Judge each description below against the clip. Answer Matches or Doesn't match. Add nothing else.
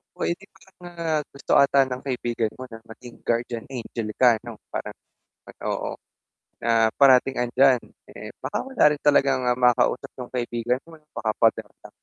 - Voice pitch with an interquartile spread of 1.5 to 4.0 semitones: Matches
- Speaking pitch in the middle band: Doesn't match